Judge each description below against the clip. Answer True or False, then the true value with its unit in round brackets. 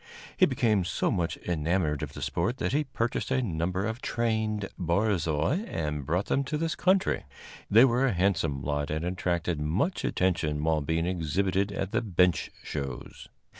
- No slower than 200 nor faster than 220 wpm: False (170 wpm)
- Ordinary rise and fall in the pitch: False (5.7 semitones)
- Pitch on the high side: False (90 Hz)